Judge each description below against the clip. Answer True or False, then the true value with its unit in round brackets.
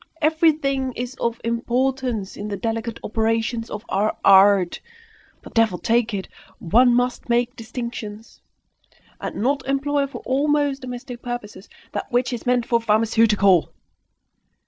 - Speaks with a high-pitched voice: True (235 Hz)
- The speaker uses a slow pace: True (130 wpm)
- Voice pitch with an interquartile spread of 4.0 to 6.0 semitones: False (2.7 semitones)